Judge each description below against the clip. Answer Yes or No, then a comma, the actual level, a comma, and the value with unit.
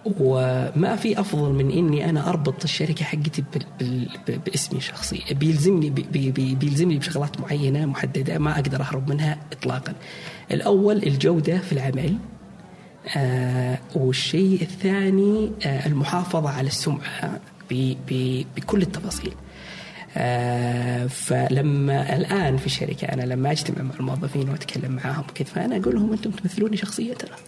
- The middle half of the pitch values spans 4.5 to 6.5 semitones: Yes, average, 5.0 semitones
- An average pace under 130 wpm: No, fast, 135 wpm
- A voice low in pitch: No, medium, 150 Hz